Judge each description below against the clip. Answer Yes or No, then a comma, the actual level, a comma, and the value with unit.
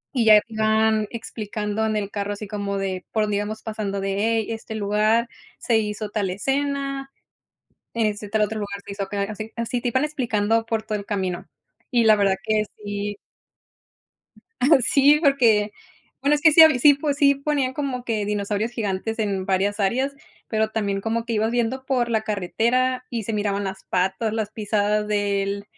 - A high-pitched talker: Yes, high, 215 Hz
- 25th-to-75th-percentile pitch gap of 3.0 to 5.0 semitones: No, narrow, 2.6 semitones